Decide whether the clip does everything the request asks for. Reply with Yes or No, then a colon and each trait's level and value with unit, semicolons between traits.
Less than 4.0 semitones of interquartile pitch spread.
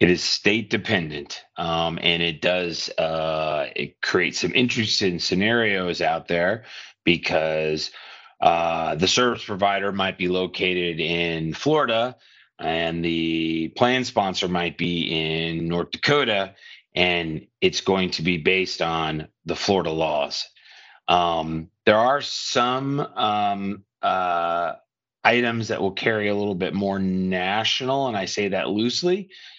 No: average, 4.5 semitones